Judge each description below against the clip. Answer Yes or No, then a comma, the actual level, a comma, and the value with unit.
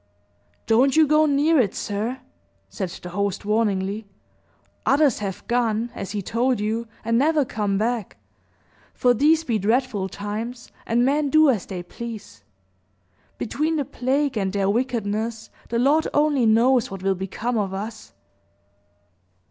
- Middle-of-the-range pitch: No, high, 230 Hz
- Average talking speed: Yes, average, 145 wpm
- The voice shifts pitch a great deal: No, average, 4.4 semitones